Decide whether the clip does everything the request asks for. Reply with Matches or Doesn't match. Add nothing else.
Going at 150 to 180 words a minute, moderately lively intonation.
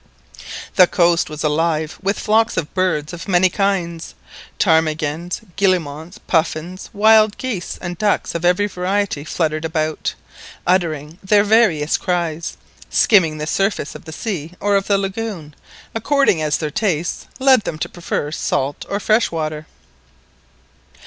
Doesn't match